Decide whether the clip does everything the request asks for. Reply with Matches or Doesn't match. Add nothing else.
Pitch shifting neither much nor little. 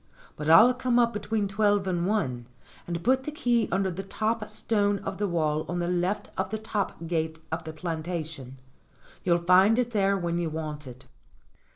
Matches